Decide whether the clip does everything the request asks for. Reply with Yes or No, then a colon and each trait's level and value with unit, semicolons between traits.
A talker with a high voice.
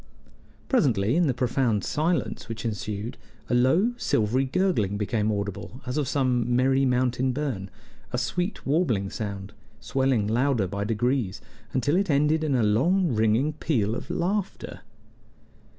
No: low, 125 Hz